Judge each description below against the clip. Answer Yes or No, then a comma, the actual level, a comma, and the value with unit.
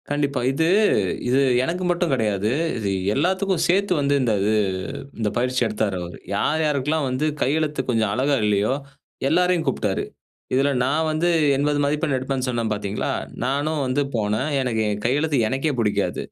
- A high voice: No, low, 135 Hz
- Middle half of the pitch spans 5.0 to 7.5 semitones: Yes, average, 5.3 semitones